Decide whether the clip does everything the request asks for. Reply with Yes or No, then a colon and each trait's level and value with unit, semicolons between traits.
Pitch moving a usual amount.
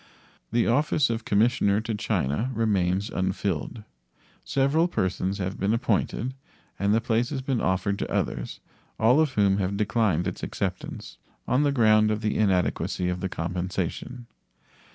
Yes: average, 4.1 semitones